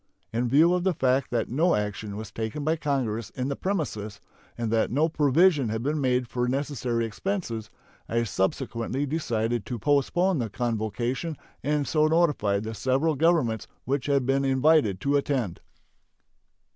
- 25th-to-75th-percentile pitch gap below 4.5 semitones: No, average, 4.8 semitones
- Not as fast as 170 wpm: Yes, average, 160 wpm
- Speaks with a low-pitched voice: Yes, low, 130 Hz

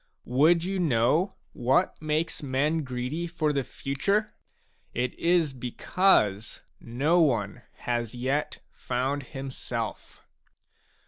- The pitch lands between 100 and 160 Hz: Yes, medium, 140 Hz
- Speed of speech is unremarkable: No, slow, 105 wpm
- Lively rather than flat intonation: No, average, 5.0 semitones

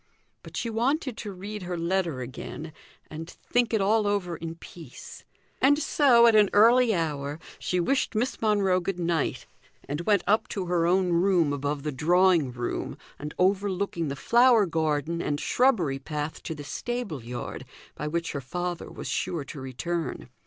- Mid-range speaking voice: Yes, medium, 175 Hz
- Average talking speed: Yes, average, 170 wpm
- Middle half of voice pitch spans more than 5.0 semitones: Yes, wide, 5.5 semitones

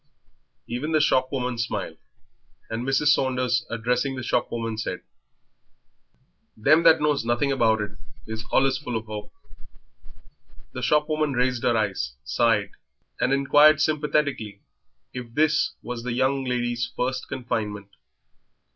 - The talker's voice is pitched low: Yes, low, 125 Hz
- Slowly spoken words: Yes, slow, 125 wpm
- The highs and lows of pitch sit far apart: No, average, 3.4 semitones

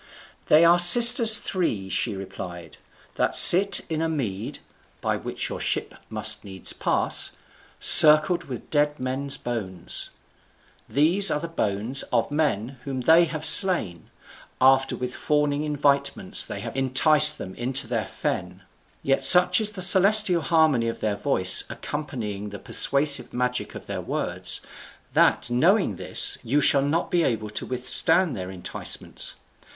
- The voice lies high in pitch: No, medium, 140 Hz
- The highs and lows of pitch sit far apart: Yes, wide, 6.1 semitones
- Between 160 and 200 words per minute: No, average, 145 wpm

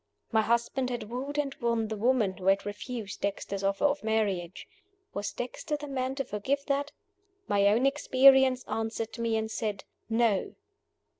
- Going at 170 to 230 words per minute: No, average, 160 wpm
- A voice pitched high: Yes, high, 230 Hz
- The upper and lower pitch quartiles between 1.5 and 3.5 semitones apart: No, average, 4.3 semitones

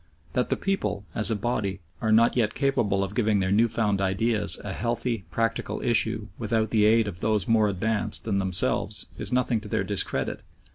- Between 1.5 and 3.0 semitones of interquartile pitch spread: Yes, narrow, 2.4 semitones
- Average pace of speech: Yes, average, 190 wpm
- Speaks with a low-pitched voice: Yes, low, 110 Hz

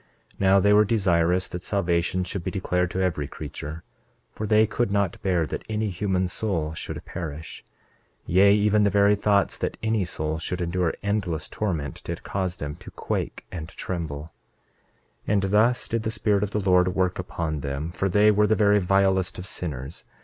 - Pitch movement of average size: Yes, average, 3.4 semitones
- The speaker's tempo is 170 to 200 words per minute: Yes, average, 185 wpm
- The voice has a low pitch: Yes, very low, 95 Hz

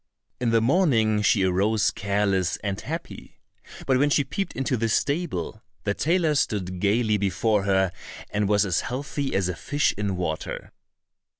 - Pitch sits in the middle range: No, low, 105 Hz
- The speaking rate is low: No, average, 160 wpm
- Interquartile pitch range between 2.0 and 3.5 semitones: No, average, 5.1 semitones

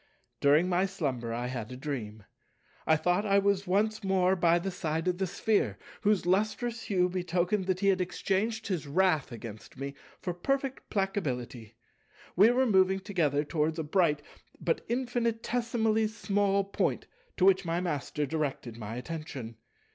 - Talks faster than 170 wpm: No, average, 155 wpm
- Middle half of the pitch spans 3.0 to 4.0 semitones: No, average, 5.3 semitones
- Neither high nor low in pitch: Yes, medium, 180 Hz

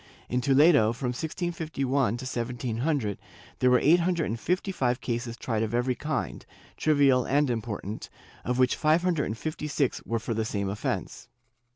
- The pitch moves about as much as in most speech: Yes, average, 4.5 semitones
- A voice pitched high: No, low, 125 Hz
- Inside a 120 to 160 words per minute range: No, average, 170 wpm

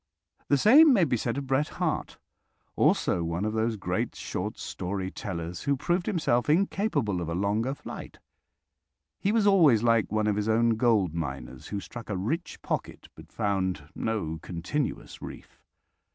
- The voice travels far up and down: Yes, wide, 7.3 semitones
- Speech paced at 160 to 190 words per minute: Yes, average, 165 wpm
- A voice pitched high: No, low, 110 Hz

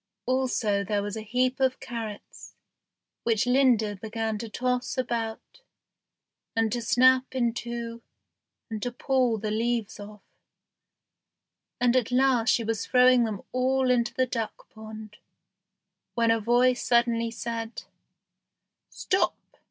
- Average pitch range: No, narrow, 2.3 semitones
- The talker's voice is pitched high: Yes, high, 235 Hz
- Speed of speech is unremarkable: No, slow, 130 wpm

